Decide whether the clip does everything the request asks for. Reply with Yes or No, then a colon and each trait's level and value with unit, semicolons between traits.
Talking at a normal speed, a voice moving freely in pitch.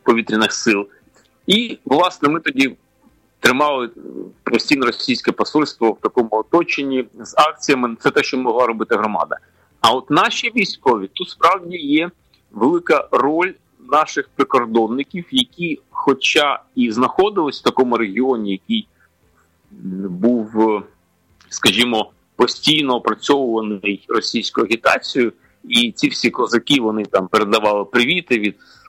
Yes: average, 115 wpm; wide, 8.4 semitones